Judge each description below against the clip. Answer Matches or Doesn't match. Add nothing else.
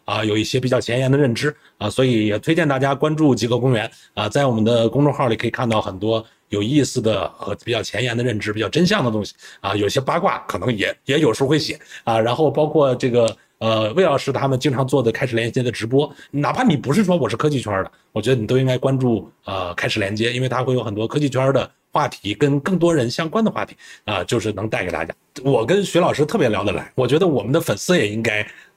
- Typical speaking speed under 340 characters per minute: Doesn't match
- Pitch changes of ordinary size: Matches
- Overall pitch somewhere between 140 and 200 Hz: Doesn't match